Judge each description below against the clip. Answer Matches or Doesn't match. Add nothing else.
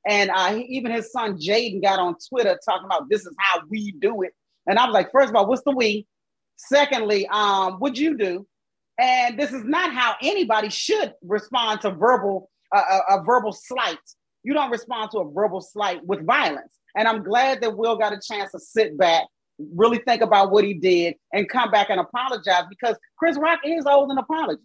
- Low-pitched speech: Doesn't match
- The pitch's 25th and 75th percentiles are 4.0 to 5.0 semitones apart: Matches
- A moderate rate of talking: Doesn't match